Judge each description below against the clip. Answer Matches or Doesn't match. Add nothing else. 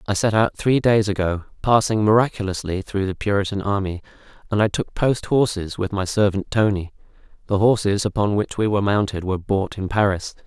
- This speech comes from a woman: Doesn't match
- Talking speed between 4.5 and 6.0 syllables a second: Matches